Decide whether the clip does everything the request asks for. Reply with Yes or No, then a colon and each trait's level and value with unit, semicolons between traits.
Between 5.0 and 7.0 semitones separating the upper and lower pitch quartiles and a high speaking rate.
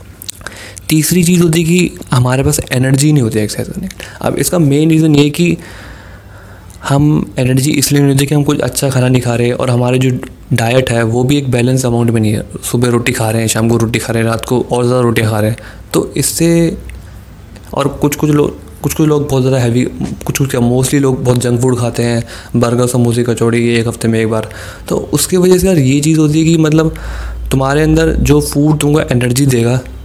No: average, 4.4 semitones; fast, 220 wpm